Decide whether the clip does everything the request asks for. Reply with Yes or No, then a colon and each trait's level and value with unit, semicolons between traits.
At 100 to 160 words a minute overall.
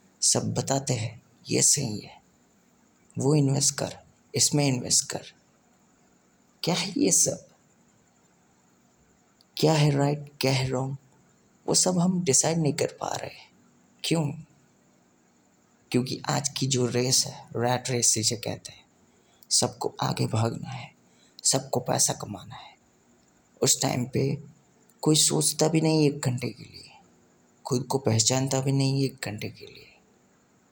Yes: average, 140 wpm